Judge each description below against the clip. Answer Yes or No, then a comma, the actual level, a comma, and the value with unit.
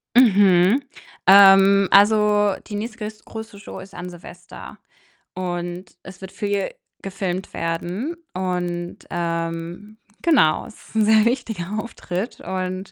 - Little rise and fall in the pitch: No, average, 3.0 semitones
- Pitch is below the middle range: No, high, 195 Hz